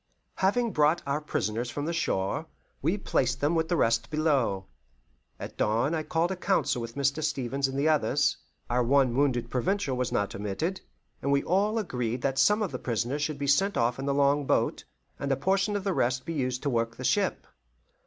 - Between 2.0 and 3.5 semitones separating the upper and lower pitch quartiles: No, average, 4.7 semitones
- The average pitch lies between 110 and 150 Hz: Yes, medium, 140 Hz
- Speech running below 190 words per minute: No, fast, 205 wpm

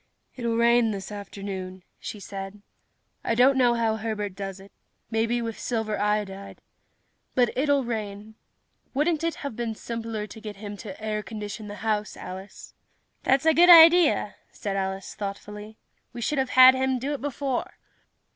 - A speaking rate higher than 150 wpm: Yes, average, 160 wpm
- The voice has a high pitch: Yes, high, 220 Hz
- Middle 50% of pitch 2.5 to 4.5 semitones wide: Yes, average, 3.6 semitones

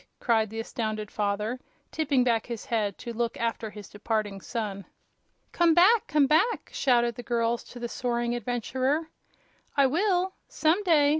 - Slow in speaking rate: No, average, 155 wpm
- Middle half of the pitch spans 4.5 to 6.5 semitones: Yes, average, 4.8 semitones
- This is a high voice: Yes, high, 240 Hz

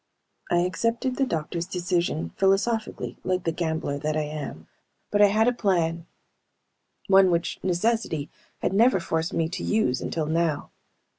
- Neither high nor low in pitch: Yes, medium, 175 Hz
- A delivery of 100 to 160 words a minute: Yes, average, 150 wpm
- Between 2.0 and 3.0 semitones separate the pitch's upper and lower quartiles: No, average, 4.3 semitones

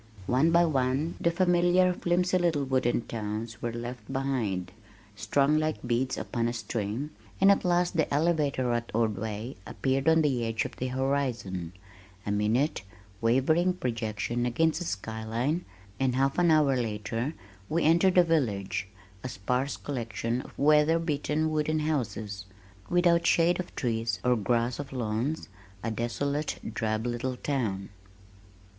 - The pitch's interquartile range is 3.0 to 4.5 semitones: No, wide, 5.5 semitones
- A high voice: No, low, 130 Hz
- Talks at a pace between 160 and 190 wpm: No, average, 145 wpm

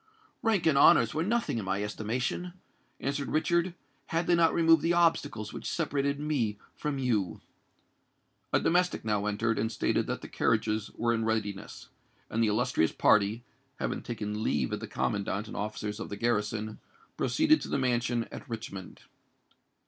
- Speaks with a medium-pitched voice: No, low, 115 Hz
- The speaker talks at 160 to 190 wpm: Yes, average, 165 wpm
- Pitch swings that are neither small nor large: No, wide, 6.2 semitones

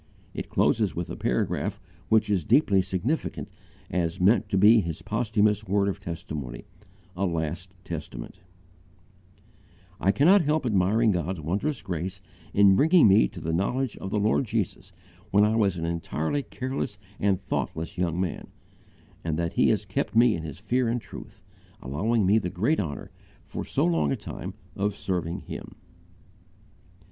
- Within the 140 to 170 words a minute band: Yes, average, 160 wpm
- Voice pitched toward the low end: Yes, very low, 95 Hz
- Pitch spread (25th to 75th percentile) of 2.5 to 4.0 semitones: No, average, 4.7 semitones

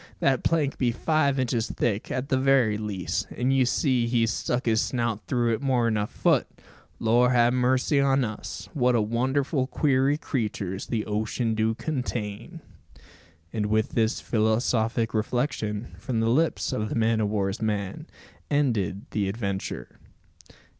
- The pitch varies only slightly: No, average, 3.2 semitones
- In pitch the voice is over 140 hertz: No, low, 120 Hz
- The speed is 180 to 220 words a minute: No, average, 150 wpm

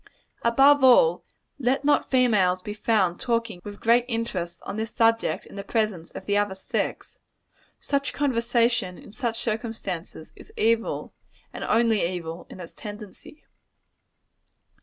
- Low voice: No, high, 225 Hz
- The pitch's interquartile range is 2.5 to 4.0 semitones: Yes, average, 3.7 semitones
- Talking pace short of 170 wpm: Yes, average, 140 wpm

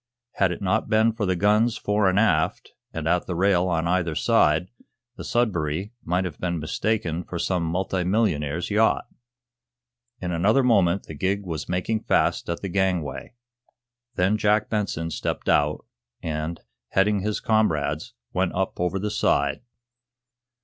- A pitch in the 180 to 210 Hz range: No, very low, 90 Hz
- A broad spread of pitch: No, average, 3.7 semitones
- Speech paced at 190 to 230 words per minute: No, average, 155 wpm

